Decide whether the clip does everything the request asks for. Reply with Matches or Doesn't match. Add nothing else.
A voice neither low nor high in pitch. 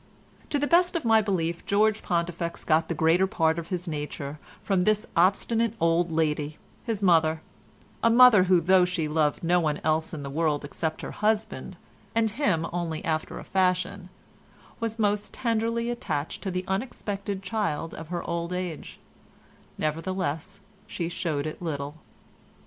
Matches